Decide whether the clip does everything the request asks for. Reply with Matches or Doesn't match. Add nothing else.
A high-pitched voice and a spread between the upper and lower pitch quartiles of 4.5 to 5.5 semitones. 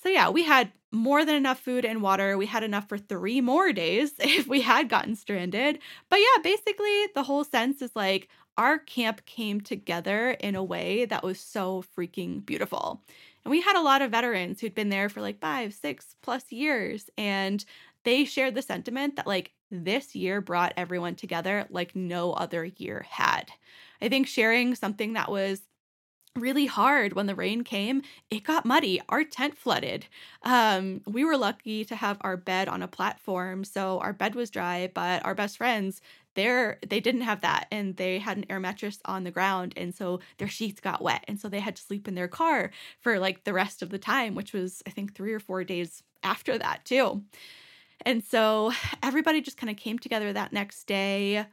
Matches